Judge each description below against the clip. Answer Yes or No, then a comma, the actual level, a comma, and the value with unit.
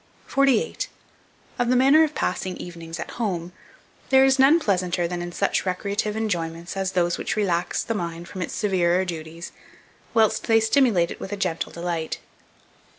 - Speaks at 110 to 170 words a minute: Yes, average, 165 wpm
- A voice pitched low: No, medium, 185 Hz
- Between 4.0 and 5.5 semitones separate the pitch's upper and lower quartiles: Yes, average, 4.6 semitones